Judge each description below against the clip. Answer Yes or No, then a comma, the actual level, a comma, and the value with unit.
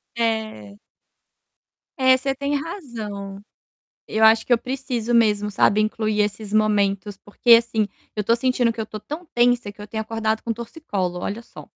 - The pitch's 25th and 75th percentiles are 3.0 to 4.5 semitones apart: No, narrow, 2.5 semitones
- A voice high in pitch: Yes, high, 220 Hz